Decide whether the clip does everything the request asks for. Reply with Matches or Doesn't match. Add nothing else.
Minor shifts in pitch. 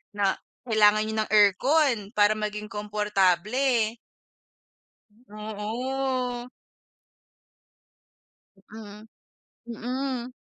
Doesn't match